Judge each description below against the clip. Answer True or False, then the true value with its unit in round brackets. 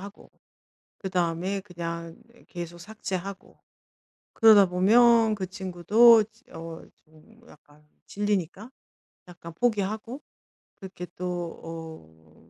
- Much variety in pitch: False (4.0 semitones)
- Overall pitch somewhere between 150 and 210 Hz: True (185 Hz)